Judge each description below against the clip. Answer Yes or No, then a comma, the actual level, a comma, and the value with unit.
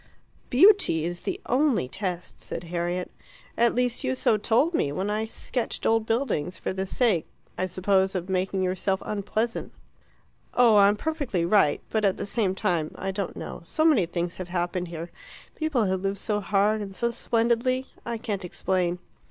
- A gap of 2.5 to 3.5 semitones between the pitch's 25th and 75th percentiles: No, average, 4.4 semitones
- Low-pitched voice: No, high, 195 Hz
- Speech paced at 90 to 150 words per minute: No, average, 175 wpm